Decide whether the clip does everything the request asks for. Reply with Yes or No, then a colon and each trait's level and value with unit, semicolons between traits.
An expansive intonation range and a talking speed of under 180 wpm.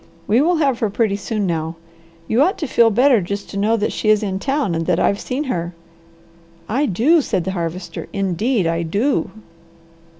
No: wide, 5.8 semitones; average, 195 wpm